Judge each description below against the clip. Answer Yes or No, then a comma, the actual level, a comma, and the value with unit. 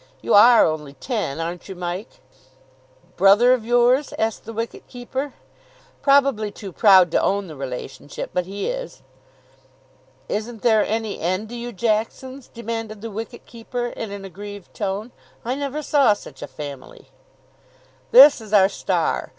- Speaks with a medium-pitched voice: No, high, 215 Hz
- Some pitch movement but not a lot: Yes, average, 4.0 semitones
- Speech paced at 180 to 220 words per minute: No, average, 150 wpm